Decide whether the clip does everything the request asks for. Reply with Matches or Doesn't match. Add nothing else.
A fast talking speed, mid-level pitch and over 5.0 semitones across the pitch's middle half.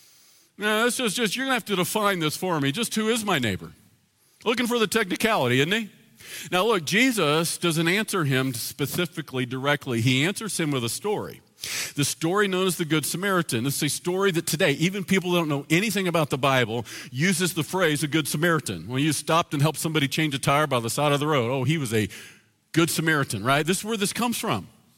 Matches